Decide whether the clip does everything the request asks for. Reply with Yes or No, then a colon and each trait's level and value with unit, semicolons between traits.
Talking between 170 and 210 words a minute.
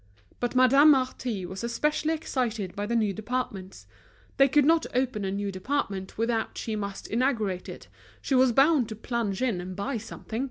Yes: average, 175 wpm